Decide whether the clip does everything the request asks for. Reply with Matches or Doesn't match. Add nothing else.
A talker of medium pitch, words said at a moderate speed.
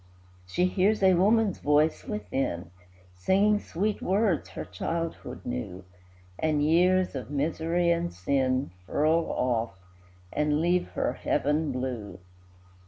Doesn't match